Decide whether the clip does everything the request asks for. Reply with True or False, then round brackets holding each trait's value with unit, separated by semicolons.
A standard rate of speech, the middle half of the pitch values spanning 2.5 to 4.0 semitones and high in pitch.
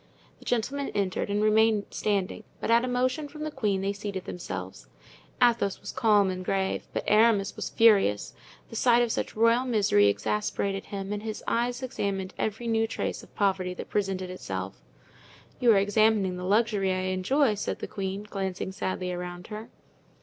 True (175 wpm; 3.2 semitones; 205 Hz)